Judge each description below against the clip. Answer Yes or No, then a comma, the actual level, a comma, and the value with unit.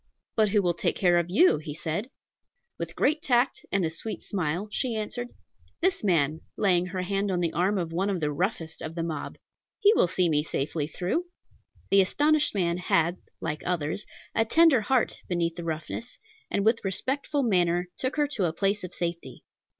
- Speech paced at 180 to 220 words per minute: Yes, average, 190 wpm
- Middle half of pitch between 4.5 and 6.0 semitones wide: Yes, average, 4.8 semitones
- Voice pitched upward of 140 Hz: Yes, medium, 185 Hz